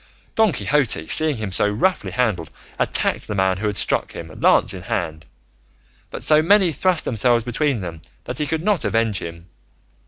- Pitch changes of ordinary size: No, wide, 8.6 semitones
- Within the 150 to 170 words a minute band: No, average, 180 wpm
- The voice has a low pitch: Yes, low, 115 Hz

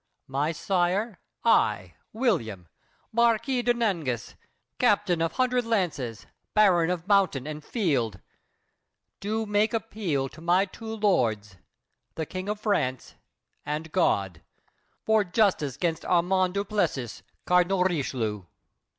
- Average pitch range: No, wide, 6.8 semitones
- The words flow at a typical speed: No, slow, 115 wpm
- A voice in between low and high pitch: Yes, medium, 180 Hz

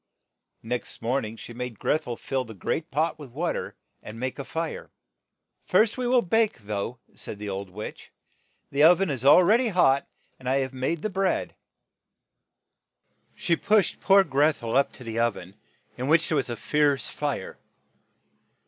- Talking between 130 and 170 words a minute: No, average, 185 wpm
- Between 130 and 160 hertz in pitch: Yes, medium, 140 Hz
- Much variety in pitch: Yes, wide, 6.2 semitones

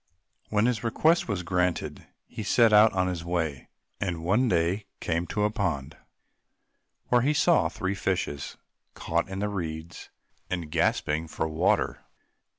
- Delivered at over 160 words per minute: No, average, 150 wpm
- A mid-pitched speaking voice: No, very low, 90 Hz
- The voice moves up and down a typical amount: Yes, average, 4.3 semitones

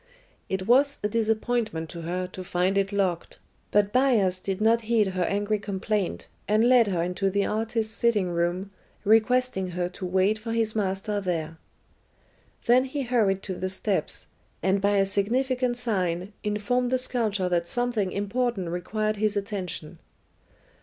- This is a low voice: No, high, 205 Hz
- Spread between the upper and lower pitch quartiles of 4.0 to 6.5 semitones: No, average, 3.5 semitones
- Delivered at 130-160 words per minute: Yes, average, 155 wpm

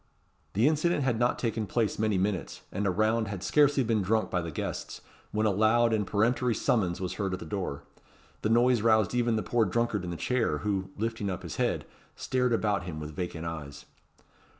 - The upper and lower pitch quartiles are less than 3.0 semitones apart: No, average, 4.1 semitones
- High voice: No, low, 110 Hz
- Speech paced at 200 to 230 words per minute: Yes, fast, 205 wpm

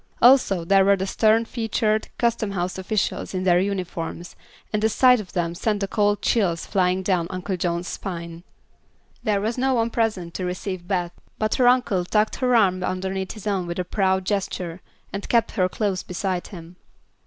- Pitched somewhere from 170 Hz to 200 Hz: Yes, high, 190 Hz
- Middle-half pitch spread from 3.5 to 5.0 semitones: No, average, 3.1 semitones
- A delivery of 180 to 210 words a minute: Yes, average, 185 wpm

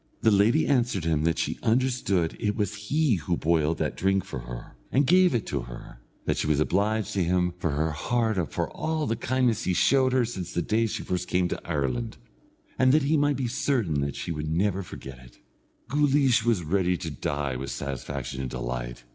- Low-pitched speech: Yes, very low, 90 Hz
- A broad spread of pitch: Yes, wide, 8.2 semitones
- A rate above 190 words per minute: Yes, fast, 205 wpm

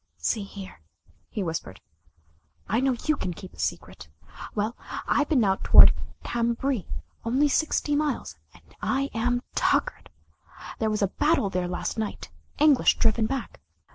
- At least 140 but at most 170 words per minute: Yes, average, 145 wpm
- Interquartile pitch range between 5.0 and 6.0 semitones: Yes, wide, 5.5 semitones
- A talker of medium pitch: No, high, 230 Hz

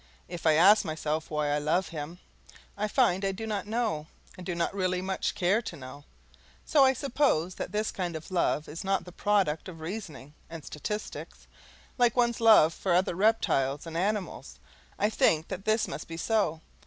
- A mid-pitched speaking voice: Yes, medium, 180 Hz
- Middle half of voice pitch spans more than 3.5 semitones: Yes, average, 5.0 semitones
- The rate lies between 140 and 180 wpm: No, average, 190 wpm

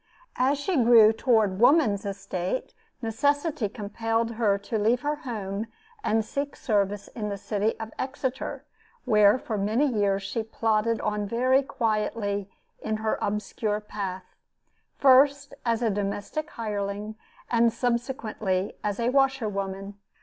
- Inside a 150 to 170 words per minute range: No, slow, 135 wpm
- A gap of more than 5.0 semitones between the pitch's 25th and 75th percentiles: No, average, 3.3 semitones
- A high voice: Yes, high, 220 Hz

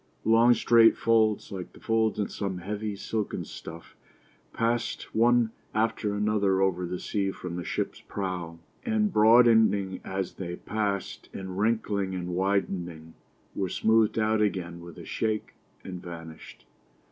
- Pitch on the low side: Yes, low, 100 Hz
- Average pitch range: Yes, average, 3.4 semitones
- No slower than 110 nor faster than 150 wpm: Yes, average, 140 wpm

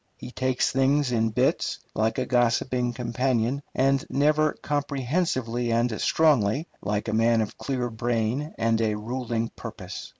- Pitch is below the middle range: Yes, low, 120 Hz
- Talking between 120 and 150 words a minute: Yes, average, 140 wpm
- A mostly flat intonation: No, average, 3.0 semitones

